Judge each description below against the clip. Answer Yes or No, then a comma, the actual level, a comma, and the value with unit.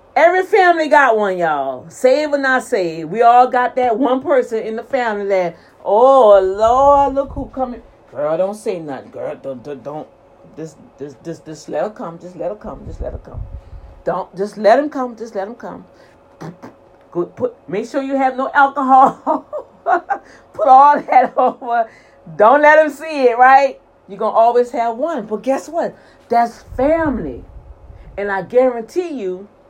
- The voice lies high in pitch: Yes, high, 240 Hz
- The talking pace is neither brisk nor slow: Yes, average, 170 wpm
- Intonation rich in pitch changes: Yes, wide, 6.4 semitones